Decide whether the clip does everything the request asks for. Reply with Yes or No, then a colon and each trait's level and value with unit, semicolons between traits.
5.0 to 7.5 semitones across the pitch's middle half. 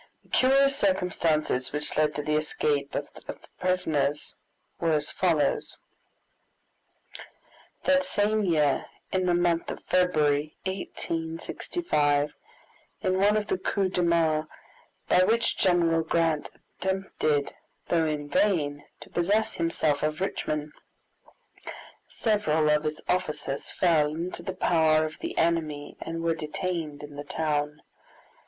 No: average, 3.4 semitones